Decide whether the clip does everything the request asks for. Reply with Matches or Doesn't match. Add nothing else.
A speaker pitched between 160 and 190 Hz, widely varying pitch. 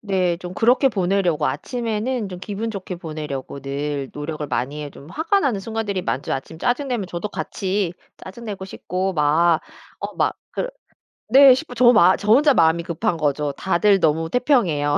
Matches